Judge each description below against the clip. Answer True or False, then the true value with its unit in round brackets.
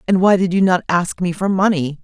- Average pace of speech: False (265 wpm)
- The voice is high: False (180 Hz)